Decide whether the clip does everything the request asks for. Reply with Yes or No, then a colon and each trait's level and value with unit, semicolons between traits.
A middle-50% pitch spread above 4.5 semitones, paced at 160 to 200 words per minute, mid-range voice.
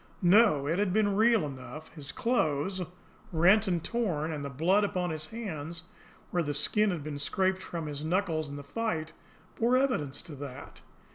Yes: wide, 5.6 semitones; average, 180 wpm; medium, 170 Hz